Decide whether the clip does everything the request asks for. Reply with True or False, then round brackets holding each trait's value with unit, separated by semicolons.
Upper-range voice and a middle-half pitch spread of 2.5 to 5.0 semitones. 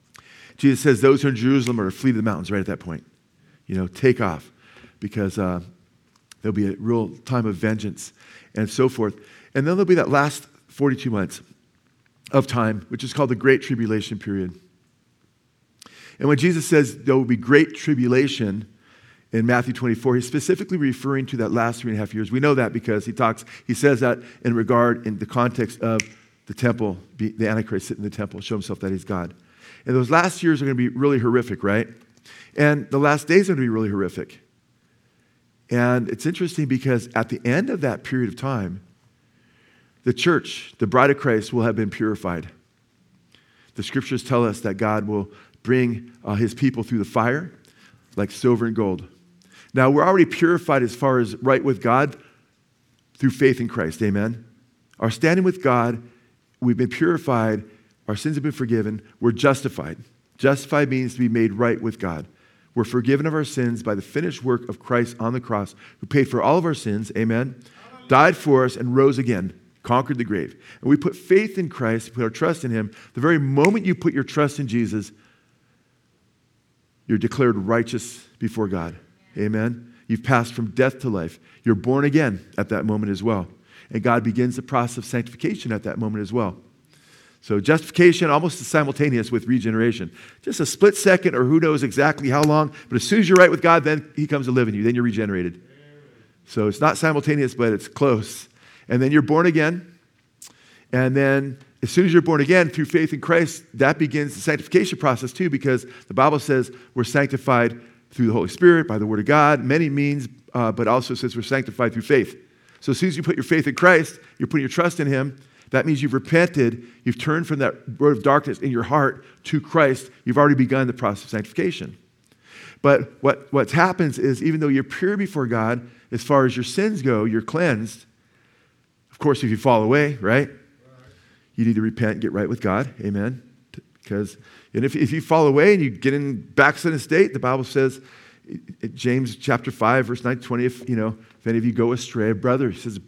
False (125 Hz; 4.1 semitones)